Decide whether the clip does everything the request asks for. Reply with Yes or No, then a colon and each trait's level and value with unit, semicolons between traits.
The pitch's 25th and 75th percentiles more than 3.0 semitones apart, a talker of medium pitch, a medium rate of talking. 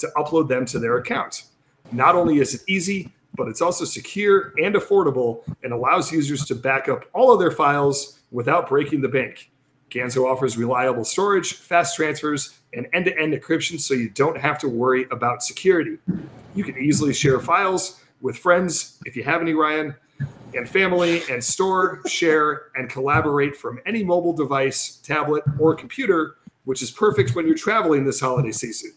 Yes: average, 4.9 semitones; medium, 150 Hz; average, 175 wpm